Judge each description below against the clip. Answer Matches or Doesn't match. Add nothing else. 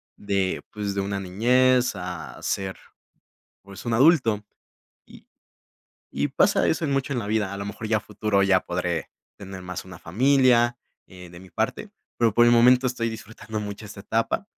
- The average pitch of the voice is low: Matches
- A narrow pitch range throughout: Doesn't match